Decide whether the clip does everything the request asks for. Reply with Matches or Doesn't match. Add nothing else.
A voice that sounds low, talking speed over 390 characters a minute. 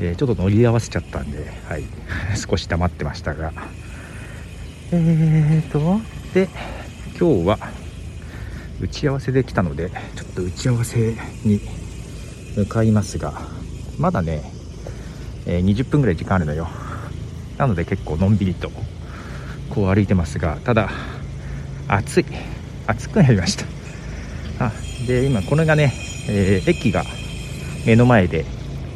Doesn't match